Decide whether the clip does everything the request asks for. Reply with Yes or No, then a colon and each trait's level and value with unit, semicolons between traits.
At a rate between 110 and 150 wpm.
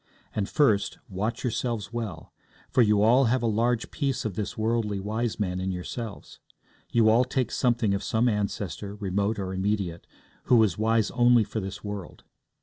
No: average, 170 wpm